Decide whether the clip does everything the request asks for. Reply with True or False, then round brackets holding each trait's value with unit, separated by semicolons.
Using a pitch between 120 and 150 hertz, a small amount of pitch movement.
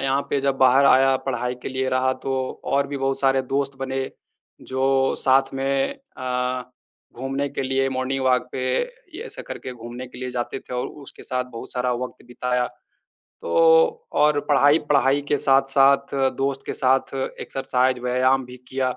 True (135 Hz; 1.1 semitones)